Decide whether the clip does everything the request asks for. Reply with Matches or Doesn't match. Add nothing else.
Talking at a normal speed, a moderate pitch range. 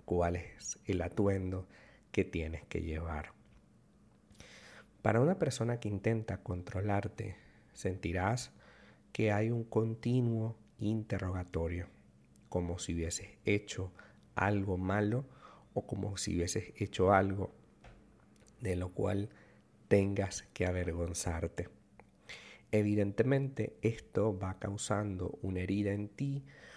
Doesn't match